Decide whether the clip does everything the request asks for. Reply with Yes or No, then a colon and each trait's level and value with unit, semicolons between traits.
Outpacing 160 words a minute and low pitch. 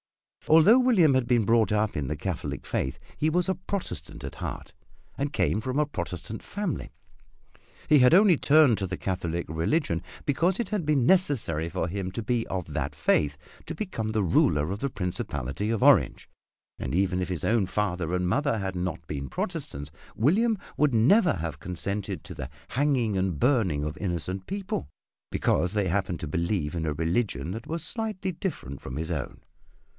Yes: average, 180 wpm; low, 100 Hz